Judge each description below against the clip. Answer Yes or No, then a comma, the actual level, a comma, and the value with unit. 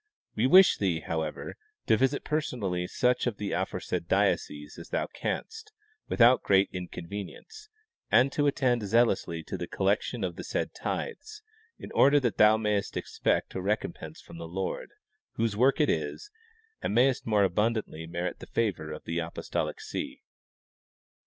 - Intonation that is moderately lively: No, wide, 6.2 semitones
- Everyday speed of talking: Yes, average, 155 wpm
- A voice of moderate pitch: No, low, 105 Hz